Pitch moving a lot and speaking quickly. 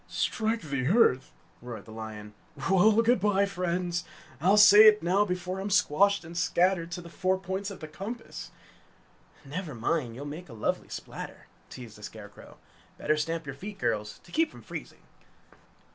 No: wide, 5.8 semitones; average, 170 wpm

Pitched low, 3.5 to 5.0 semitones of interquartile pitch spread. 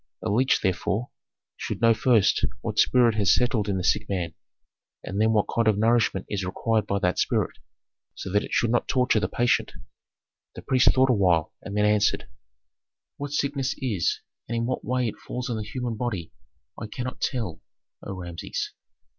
Yes: low, 110 Hz; average, 3.8 semitones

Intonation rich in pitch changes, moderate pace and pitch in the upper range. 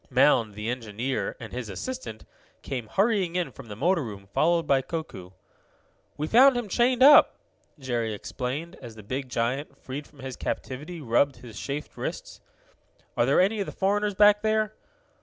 No: wide, 8.4 semitones; average, 170 wpm; medium, 140 Hz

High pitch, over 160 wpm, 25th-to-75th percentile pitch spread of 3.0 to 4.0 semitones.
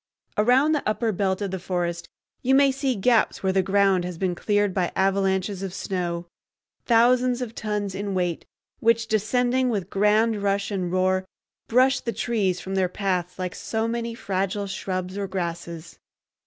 Yes: high, 200 Hz; average, 170 wpm; average, 3.6 semitones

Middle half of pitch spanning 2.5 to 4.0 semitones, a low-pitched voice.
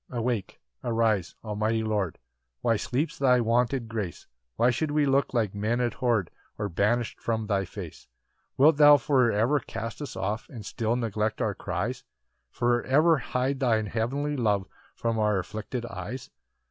Yes: average, 3.0 semitones; low, 115 Hz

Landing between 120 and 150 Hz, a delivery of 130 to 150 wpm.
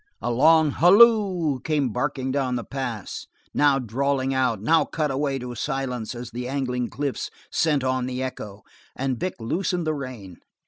No: low, 135 Hz; average, 165 wpm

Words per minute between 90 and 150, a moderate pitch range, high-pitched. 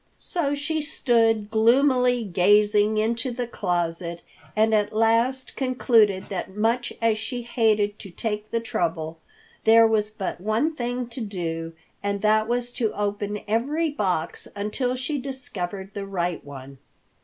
Yes: average, 145 wpm; average, 3.3 semitones; high, 220 Hz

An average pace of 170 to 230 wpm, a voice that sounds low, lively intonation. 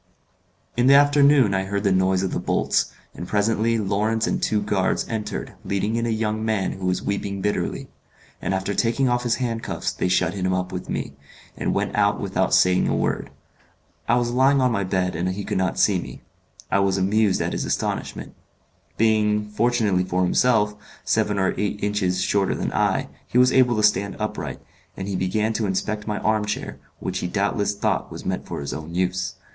No: average, 200 wpm; low, 105 Hz; average, 2.9 semitones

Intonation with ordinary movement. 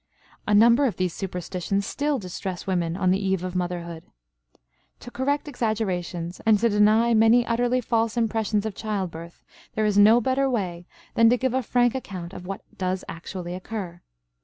Yes: average, 4.3 semitones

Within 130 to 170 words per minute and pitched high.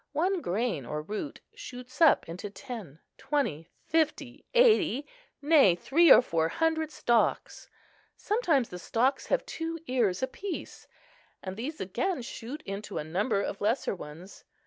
Yes: average, 140 wpm; very high, 250 Hz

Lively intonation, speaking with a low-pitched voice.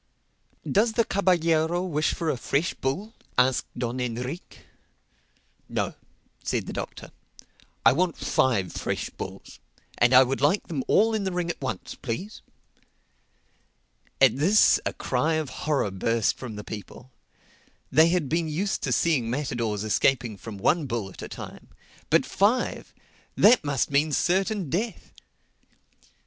No: wide, 6.4 semitones; medium, 145 Hz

